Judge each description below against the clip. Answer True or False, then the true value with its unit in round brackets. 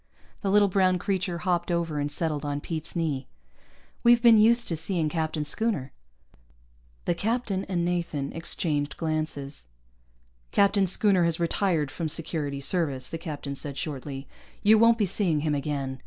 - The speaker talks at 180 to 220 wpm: False (155 wpm)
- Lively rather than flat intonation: False (4.6 semitones)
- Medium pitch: True (165 Hz)